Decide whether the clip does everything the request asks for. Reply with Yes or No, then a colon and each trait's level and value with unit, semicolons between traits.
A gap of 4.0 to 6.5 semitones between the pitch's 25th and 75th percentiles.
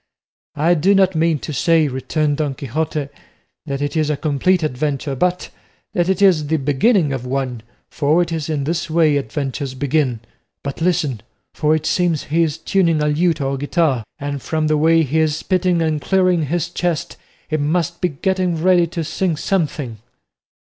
No: average, 3.2 semitones